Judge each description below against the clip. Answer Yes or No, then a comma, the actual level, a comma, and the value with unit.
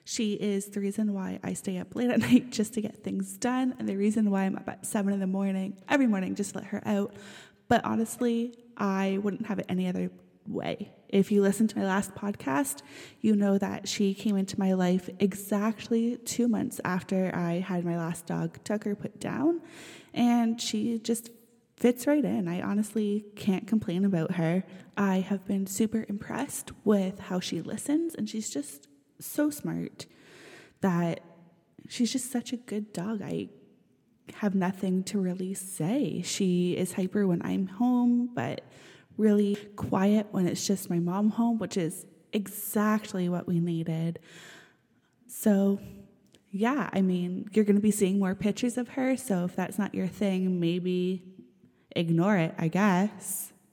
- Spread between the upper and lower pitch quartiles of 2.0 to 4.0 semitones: Yes, average, 3.2 semitones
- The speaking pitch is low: No, high, 200 Hz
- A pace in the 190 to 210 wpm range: No, average, 170 wpm